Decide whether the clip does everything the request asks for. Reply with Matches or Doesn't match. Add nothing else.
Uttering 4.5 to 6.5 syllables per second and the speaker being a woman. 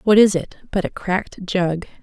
Matches